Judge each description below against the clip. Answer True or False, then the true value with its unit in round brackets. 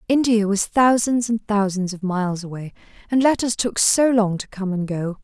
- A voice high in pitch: True (210 Hz)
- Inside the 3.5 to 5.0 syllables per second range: True (4.9 syllables/s)